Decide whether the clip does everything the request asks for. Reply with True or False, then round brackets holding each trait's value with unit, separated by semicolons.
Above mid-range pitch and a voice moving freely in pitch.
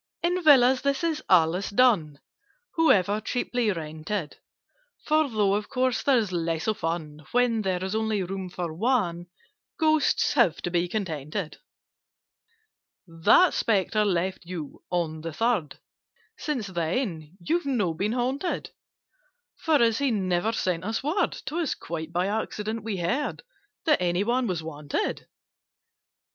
True (200 Hz; 6.4 semitones)